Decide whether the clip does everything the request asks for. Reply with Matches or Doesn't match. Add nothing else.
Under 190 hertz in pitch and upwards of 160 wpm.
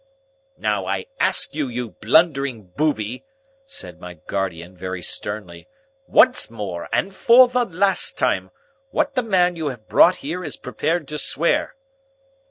Doesn't match